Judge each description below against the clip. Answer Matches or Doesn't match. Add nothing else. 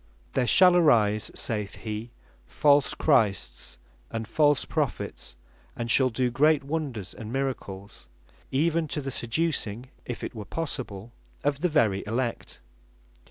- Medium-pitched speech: Doesn't match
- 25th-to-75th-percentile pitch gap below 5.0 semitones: Doesn't match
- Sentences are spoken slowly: Matches